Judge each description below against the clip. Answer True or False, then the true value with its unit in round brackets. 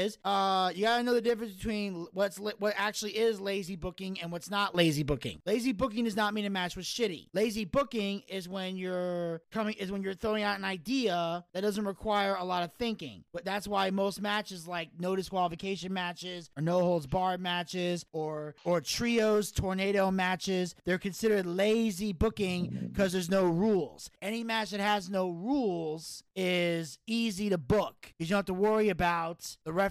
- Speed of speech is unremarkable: True (185 wpm)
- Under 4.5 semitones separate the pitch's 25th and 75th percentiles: True (2.9 semitones)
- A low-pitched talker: False (195 Hz)